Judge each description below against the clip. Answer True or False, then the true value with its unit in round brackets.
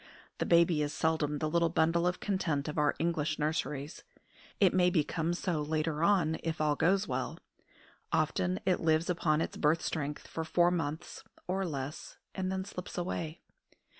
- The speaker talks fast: False (165 wpm)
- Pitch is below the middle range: False (160 Hz)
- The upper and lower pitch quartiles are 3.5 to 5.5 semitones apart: False (2.7 semitones)